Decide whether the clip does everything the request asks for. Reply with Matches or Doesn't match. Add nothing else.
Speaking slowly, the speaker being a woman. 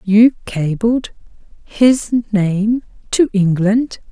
Matches